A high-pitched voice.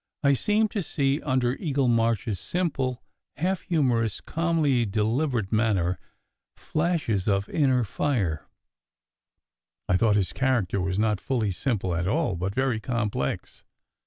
No: low, 120 Hz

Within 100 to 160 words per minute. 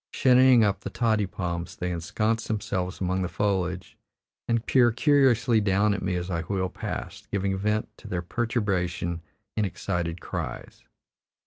Yes: average, 150 wpm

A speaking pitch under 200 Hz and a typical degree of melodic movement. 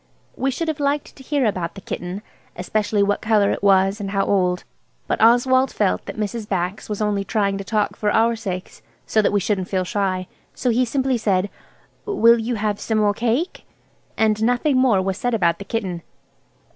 No: high, 210 Hz; average, 3.2 semitones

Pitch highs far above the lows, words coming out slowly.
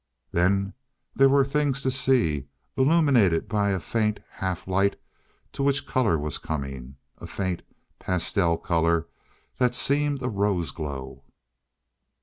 Yes: wide, 8.0 semitones; slow, 130 wpm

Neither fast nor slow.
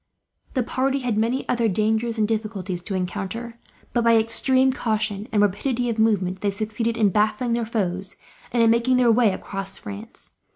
Yes: average, 175 wpm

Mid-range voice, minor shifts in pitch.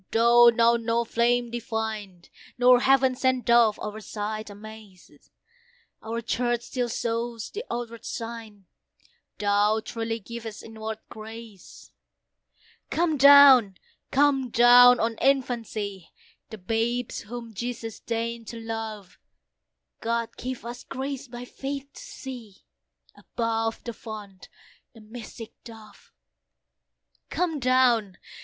No: high, 230 Hz; narrow, 2.0 semitones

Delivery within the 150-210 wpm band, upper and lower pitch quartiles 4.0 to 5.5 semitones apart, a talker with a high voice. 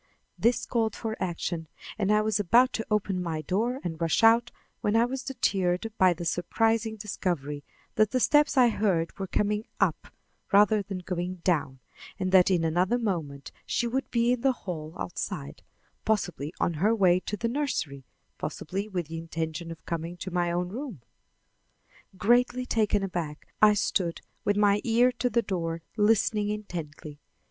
Yes: average, 170 wpm; average, 4.7 semitones; high, 195 Hz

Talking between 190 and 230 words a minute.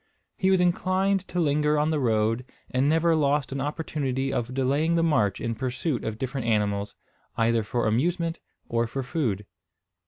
No: average, 165 wpm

